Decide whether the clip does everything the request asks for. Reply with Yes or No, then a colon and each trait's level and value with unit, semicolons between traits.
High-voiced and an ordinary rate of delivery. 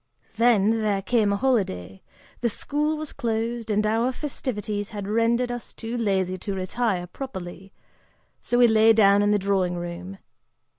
Yes: high, 215 Hz; average, 155 wpm